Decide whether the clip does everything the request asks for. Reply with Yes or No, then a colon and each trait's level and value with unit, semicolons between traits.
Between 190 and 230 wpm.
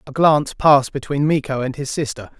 Yes: average, 200 wpm